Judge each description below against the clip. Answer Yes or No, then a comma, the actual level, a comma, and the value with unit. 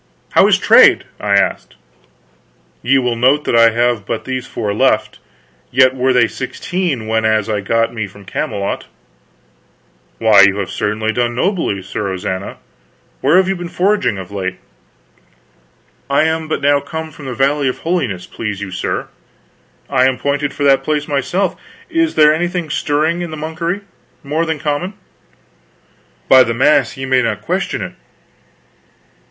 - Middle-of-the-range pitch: No, low, 130 Hz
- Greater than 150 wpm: Yes, average, 160 wpm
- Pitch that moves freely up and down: Yes, wide, 5.9 semitones